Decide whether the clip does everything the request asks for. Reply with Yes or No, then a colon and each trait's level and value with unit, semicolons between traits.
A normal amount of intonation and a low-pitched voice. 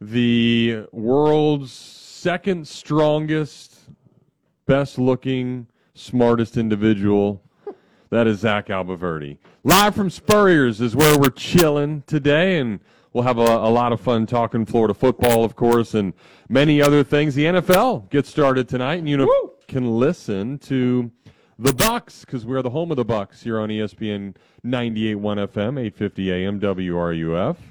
Yes: average, 5.0 semitones; low, 125 Hz